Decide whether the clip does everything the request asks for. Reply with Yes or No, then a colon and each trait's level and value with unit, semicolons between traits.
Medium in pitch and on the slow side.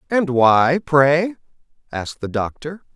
Yes: medium, 150 Hz; slow, 120 wpm